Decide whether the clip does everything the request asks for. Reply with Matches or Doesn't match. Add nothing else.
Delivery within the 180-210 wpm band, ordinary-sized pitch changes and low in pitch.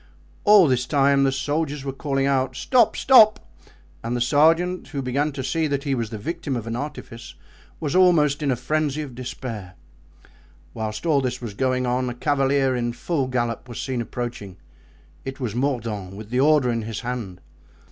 Matches